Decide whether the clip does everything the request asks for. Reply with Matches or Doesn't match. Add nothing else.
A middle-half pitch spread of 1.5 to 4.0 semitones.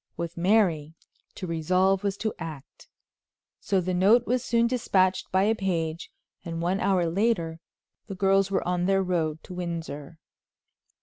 Matches